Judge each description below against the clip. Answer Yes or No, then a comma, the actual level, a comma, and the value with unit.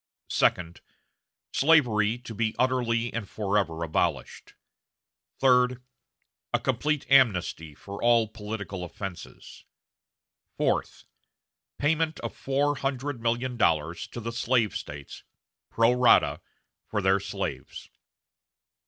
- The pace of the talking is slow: Yes, slow, 100 wpm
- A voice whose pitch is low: Yes, low, 115 Hz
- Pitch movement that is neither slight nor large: Yes, average, 4.5 semitones